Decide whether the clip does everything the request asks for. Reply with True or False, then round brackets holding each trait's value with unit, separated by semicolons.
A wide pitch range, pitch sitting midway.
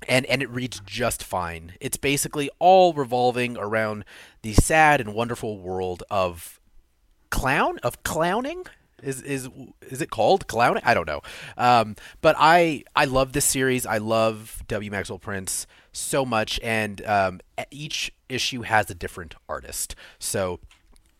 False (5.9 semitones; 110 Hz)